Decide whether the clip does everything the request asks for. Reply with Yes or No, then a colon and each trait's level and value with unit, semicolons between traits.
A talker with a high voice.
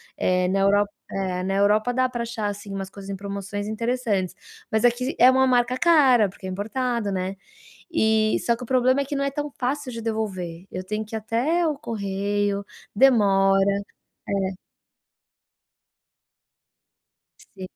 Yes: high, 215 Hz